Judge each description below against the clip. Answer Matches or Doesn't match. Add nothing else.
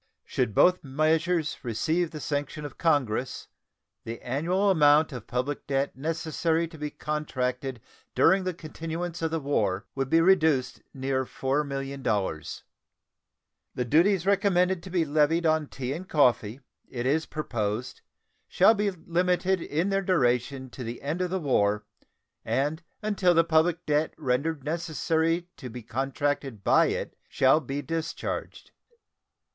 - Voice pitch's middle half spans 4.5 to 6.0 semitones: Doesn't match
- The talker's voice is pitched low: Doesn't match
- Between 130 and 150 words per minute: Matches